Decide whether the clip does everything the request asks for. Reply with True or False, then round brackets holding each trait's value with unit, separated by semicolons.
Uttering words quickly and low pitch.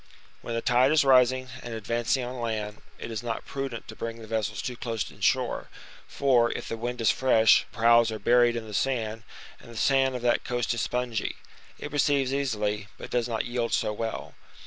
True (210 wpm; 120 Hz)